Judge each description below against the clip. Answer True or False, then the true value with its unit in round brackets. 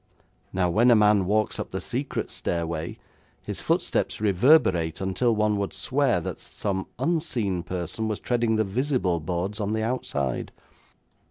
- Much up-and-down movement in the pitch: False (3.9 semitones)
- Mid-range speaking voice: False (105 Hz)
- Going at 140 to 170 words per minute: True (150 wpm)